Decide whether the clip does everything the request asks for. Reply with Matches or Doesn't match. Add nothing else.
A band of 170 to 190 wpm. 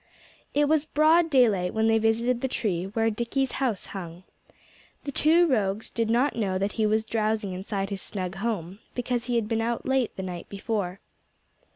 Matches